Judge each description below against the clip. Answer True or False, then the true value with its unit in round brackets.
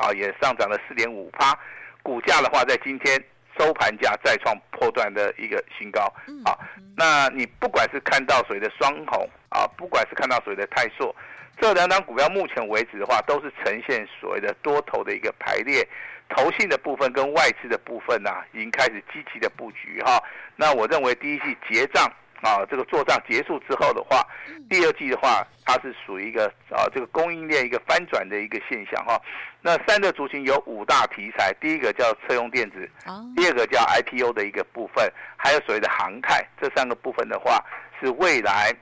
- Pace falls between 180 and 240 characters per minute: False (305 characters per minute)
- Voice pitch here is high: True (205 Hz)